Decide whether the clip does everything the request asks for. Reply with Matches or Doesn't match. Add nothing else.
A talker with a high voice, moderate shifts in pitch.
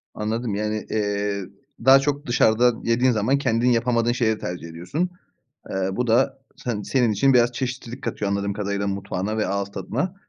Doesn't match